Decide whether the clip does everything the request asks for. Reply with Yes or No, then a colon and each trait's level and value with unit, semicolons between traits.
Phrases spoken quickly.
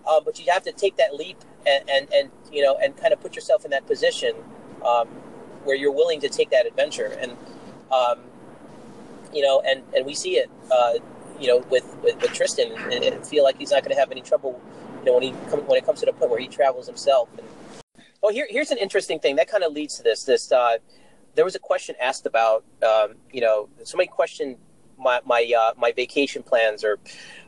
Yes: fast, 225 wpm